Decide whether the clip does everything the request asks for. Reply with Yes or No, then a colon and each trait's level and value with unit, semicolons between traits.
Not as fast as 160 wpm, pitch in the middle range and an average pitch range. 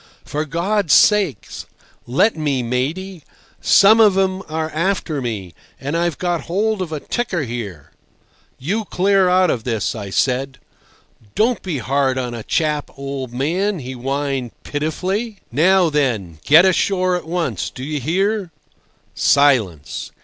No: average, 140 wpm; medium, 155 Hz; wide, 6.3 semitones